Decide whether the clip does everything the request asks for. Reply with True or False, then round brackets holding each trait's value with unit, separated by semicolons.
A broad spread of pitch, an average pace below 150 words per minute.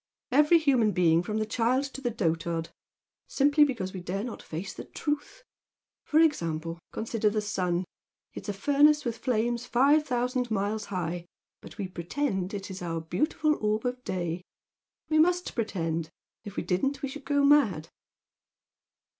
False (7.5 semitones; 165 wpm)